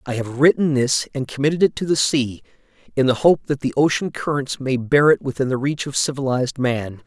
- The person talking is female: No, male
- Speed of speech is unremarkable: No, fast, 220 wpm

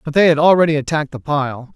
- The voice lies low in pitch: No, medium, 150 Hz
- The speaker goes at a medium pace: No, fast, 240 wpm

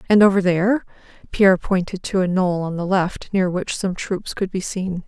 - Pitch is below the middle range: No, medium, 185 Hz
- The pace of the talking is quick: Yes, fast, 215 wpm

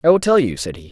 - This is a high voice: No, low, 135 Hz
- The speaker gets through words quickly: Yes, fast, 390 wpm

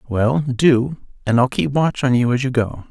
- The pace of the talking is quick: Yes, fast, 230 wpm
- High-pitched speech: No, low, 130 Hz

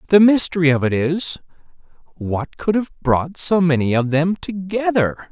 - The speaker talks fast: No, average, 160 wpm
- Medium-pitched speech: Yes, medium, 170 Hz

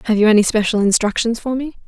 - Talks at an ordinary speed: No, fast, 225 wpm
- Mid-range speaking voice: No, high, 225 Hz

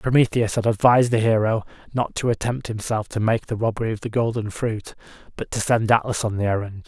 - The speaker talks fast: Yes, fast, 210 wpm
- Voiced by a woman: No, male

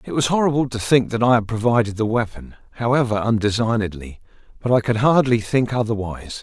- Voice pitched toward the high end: No, low, 115 Hz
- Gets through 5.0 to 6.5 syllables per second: Yes, 6.0 syllables/s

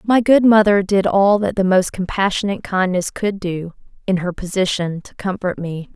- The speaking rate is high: No, average, 180 wpm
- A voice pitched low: No, high, 190 Hz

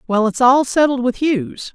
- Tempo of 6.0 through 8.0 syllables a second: No, 5.0 syllables/s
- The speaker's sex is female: Yes, female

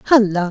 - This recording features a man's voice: No, female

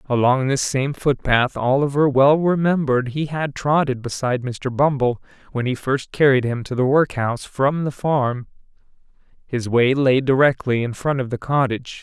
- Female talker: No, male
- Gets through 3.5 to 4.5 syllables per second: No, 4.8 syllables/s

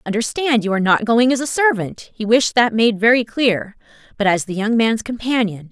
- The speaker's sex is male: No, female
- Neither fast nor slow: Yes, average, 190 wpm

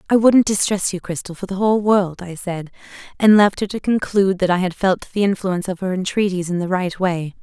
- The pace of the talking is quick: Yes, fast, 225 wpm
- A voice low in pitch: No, high, 190 Hz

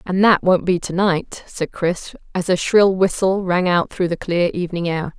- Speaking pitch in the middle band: Yes, medium, 180 Hz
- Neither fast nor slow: No, fast, 220 wpm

